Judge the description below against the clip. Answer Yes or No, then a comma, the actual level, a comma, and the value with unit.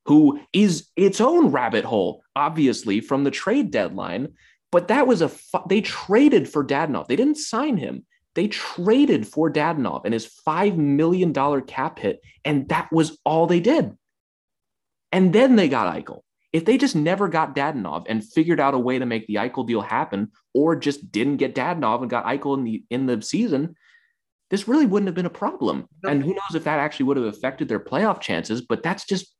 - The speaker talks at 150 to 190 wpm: No, average, 200 wpm